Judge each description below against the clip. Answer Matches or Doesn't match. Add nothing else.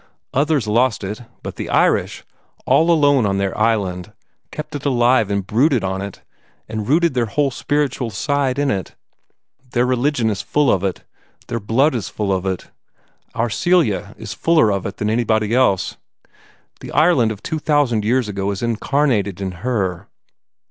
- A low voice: Matches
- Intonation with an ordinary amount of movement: Doesn't match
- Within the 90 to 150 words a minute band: Doesn't match